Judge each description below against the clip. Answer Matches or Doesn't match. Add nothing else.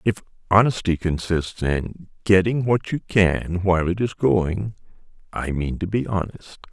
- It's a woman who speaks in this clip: Doesn't match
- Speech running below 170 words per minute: Matches